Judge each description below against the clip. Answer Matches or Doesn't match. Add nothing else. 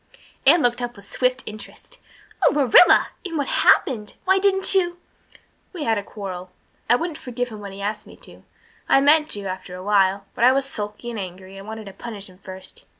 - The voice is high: Matches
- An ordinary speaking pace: Doesn't match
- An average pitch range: Doesn't match